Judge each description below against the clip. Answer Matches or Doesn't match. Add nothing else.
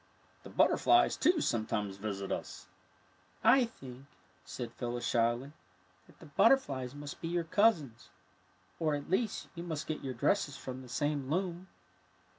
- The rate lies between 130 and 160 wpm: Matches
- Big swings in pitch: Matches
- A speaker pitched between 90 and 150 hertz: Matches